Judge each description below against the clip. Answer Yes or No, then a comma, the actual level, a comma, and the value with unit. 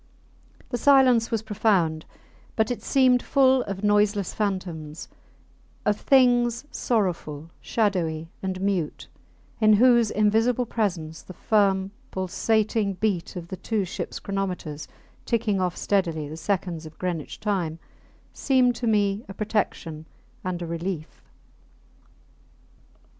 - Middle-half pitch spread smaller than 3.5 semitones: No, average, 4.3 semitones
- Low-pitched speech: No, high, 200 Hz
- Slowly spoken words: Yes, slow, 120 wpm